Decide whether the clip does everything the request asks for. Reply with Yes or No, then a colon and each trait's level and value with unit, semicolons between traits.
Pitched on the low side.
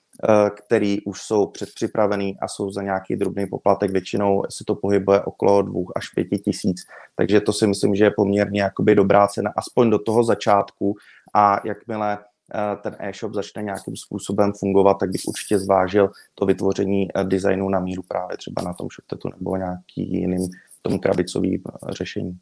Yes: low, 100 Hz